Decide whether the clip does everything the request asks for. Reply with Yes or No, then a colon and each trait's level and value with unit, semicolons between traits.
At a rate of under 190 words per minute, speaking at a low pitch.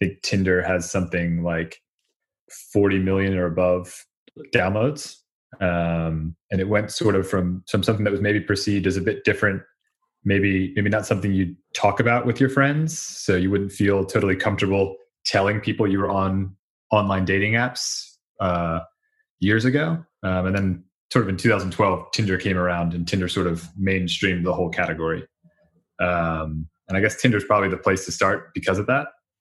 Yes: average, 180 wpm; very low, 95 Hz